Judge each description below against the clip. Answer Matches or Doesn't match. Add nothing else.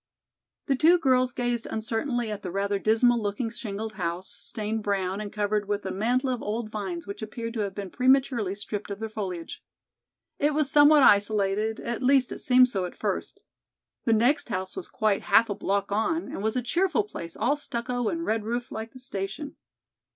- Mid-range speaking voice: Doesn't match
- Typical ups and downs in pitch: Matches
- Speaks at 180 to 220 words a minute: Matches